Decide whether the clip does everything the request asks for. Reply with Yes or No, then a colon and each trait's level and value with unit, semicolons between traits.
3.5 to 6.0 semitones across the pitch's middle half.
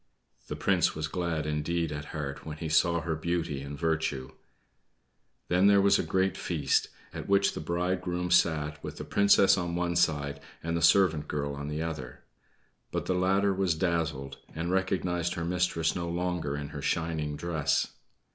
No: average, 2.8 semitones